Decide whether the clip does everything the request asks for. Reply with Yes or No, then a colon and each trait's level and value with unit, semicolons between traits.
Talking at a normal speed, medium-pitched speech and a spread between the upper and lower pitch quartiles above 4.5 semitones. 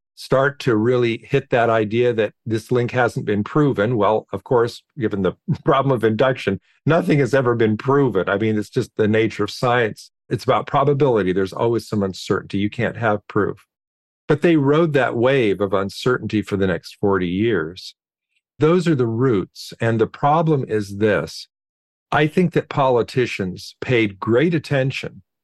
No: average, 170 wpm; low, 115 Hz; average, 4.9 semitones